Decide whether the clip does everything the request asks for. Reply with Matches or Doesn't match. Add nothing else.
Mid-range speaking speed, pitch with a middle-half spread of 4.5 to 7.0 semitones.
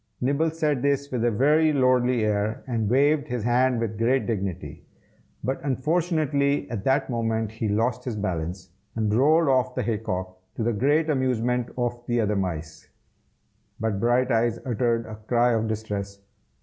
Doesn't match